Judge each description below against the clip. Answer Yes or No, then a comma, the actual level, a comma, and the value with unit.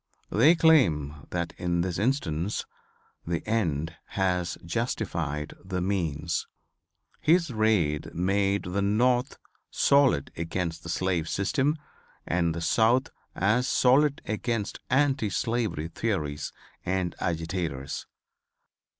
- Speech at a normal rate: No, slow, 105 wpm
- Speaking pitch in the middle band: No, very low, 95 Hz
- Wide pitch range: Yes, wide, 5.8 semitones